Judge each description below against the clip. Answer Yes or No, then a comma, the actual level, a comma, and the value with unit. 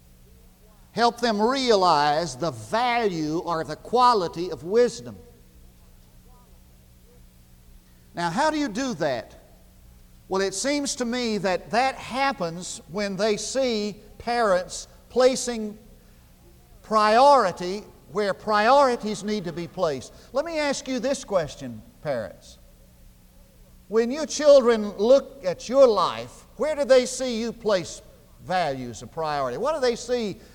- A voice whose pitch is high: Yes, high, 195 Hz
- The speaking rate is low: Yes, slow, 125 wpm